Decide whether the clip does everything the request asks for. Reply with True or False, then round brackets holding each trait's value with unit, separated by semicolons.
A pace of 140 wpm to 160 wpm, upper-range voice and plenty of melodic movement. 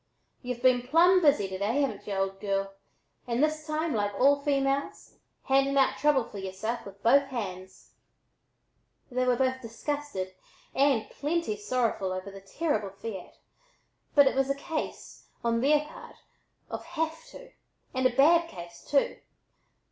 True (155 wpm; 255 Hz; 6.0 semitones)